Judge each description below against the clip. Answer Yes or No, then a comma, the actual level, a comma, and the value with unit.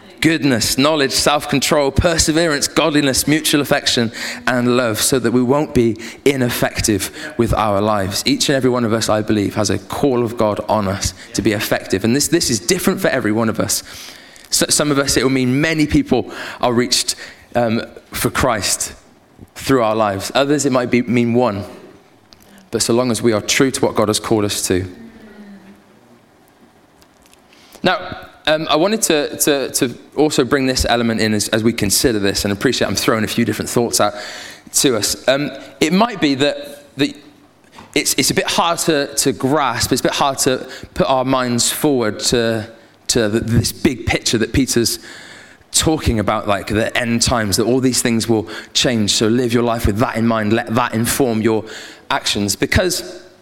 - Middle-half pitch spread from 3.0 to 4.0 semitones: No, average, 4.5 semitones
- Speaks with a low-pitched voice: Yes, low, 120 Hz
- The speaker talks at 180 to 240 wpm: Yes, average, 190 wpm